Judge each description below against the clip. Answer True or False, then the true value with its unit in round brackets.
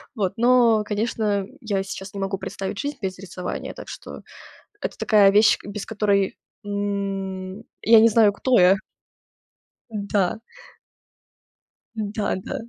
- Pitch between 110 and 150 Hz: False (205 Hz)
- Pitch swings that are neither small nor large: False (2.1 semitones)